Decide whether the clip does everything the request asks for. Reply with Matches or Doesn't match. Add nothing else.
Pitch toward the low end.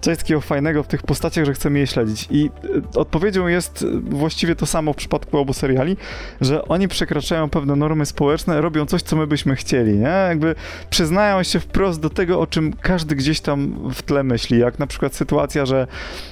Doesn't match